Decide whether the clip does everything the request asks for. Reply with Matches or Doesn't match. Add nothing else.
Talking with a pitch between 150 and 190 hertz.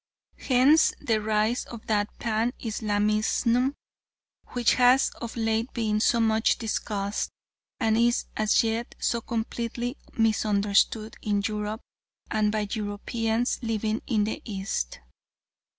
Doesn't match